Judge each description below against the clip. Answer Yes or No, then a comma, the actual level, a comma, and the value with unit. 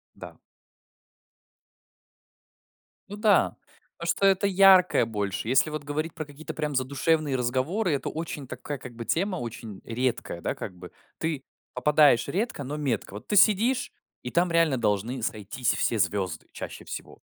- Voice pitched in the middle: Yes, medium, 145 Hz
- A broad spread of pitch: Yes, wide, 6.1 semitones